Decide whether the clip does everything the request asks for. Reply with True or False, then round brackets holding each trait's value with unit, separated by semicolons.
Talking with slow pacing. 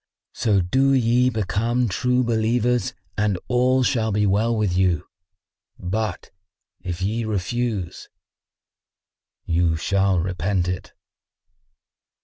True (105 wpm)